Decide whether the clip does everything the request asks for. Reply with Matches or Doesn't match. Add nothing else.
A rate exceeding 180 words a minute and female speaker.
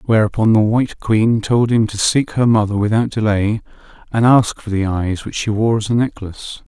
Doesn't match